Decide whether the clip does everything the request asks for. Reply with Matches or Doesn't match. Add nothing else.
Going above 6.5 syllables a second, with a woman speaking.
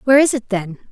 Matches